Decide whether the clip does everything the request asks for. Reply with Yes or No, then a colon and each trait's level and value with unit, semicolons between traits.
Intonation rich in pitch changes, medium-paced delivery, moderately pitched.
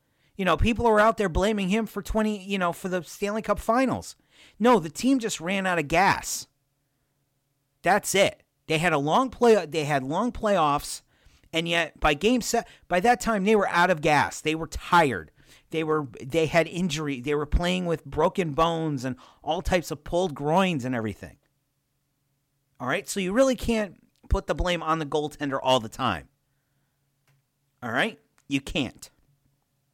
Yes: wide, 5.9 semitones; average, 180 wpm; medium, 160 Hz